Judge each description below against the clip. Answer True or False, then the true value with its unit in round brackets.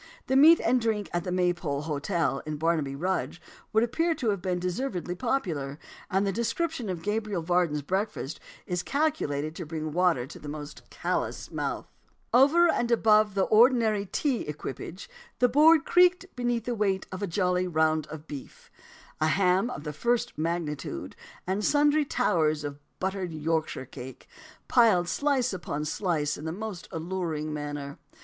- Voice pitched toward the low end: False (180 Hz)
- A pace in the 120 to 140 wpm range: False (160 wpm)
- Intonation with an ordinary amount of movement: False (6.8 semitones)